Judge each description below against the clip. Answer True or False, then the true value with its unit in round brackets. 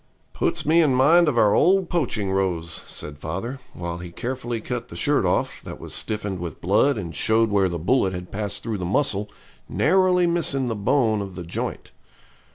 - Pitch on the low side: True (110 Hz)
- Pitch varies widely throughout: True (6.7 semitones)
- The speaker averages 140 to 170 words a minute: False (190 wpm)